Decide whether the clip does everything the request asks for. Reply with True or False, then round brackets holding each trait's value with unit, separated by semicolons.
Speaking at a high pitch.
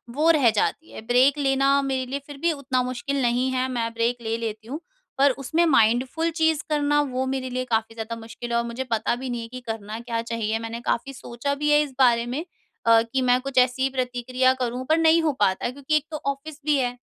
True (255 Hz)